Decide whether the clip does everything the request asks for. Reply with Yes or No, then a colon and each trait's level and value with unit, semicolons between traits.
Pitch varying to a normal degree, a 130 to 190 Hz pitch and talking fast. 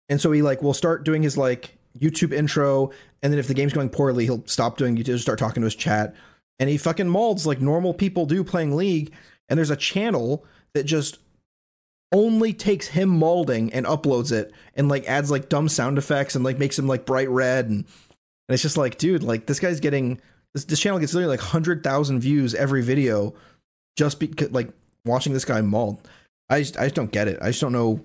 Yes: average, 4.0 semitones; medium, 140 Hz; fast, 220 wpm